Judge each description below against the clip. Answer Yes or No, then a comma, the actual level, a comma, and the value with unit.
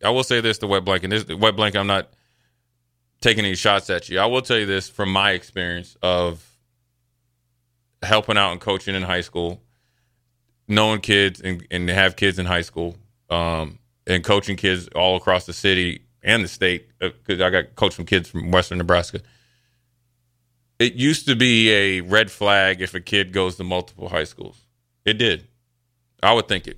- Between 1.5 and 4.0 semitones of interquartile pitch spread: No, average, 4.7 semitones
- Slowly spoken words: No, average, 190 wpm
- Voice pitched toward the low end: Yes, low, 100 Hz